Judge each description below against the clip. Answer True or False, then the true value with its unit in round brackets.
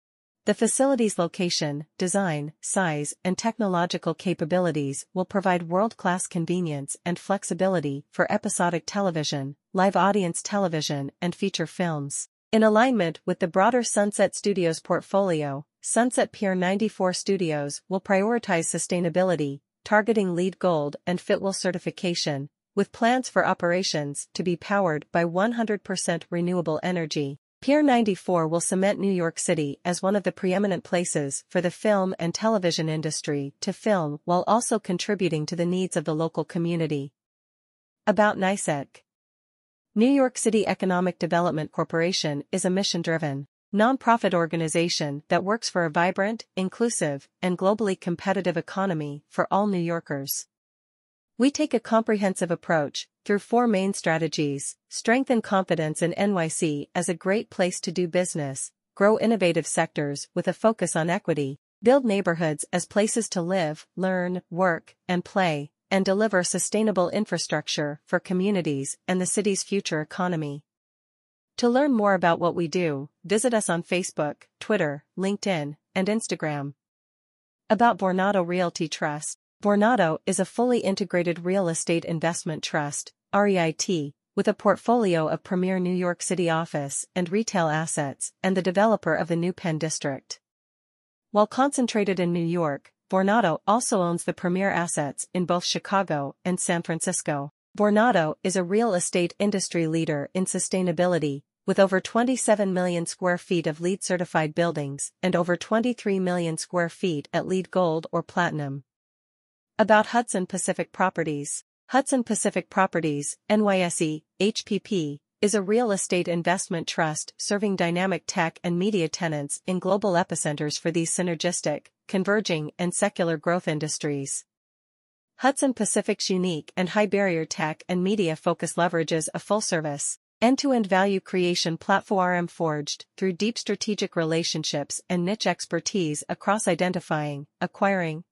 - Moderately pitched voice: True (180 Hz)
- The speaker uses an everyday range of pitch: True (3.4 semitones)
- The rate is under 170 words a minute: True (140 wpm)